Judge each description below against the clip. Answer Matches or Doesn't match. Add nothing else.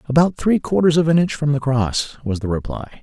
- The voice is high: Doesn't match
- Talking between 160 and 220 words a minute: Doesn't match